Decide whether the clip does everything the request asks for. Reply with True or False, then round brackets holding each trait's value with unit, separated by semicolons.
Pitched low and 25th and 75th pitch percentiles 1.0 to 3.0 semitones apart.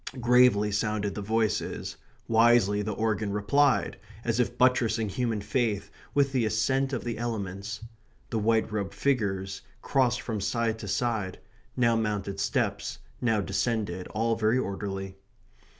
True (110 Hz; 2.7 semitones)